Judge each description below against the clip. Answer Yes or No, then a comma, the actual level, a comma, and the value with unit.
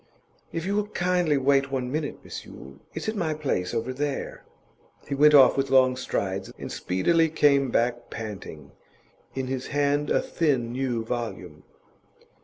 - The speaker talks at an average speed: Yes, average, 160 wpm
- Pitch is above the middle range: No, low, 135 Hz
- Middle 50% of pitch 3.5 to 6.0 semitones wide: Yes, average, 3.9 semitones